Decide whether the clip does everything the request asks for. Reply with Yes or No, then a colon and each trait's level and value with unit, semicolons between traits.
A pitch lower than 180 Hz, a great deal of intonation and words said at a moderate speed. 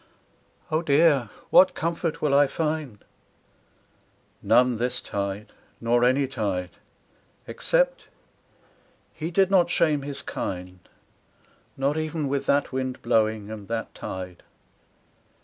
No: low, 135 Hz; wide, 6.1 semitones; slow, 120 wpm